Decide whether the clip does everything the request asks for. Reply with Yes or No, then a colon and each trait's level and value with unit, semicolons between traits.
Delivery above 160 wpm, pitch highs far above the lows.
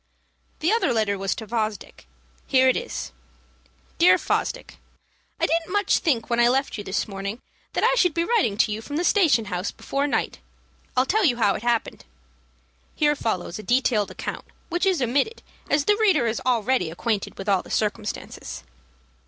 Yes: average, 185 wpm; wide, 6.9 semitones